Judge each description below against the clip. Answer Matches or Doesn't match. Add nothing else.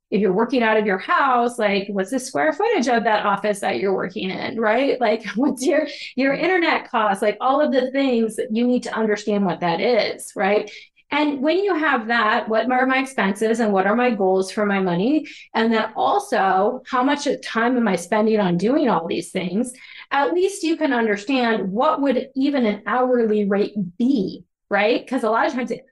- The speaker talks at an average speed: Doesn't match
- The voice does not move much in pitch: Doesn't match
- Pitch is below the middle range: Doesn't match